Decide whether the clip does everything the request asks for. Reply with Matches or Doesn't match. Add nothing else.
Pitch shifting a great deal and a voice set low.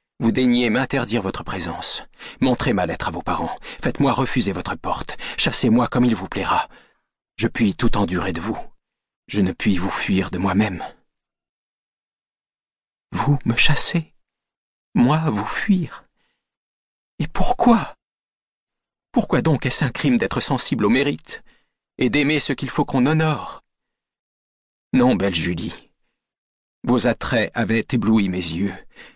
Matches